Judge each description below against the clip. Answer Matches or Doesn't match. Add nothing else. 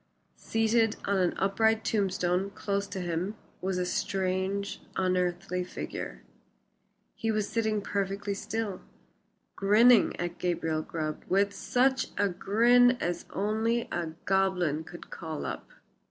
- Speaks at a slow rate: Matches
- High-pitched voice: Matches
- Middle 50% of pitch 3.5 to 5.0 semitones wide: Doesn't match